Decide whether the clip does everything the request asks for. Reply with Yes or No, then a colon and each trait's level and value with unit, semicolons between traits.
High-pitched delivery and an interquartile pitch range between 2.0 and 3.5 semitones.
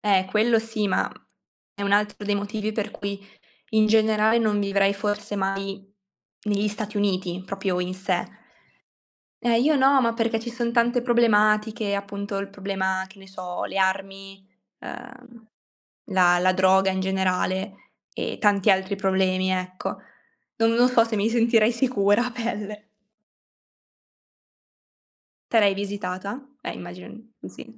Yes: high, 205 Hz; average, 2.7 semitones